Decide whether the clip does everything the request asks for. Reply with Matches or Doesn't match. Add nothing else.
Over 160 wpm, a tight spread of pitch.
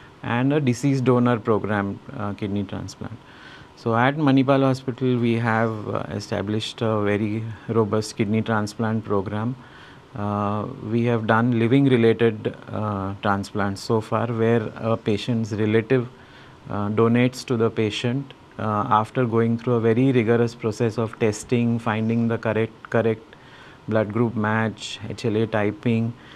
Doesn't match